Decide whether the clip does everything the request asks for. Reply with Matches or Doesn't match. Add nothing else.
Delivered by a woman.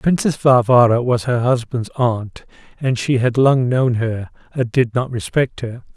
Doesn't match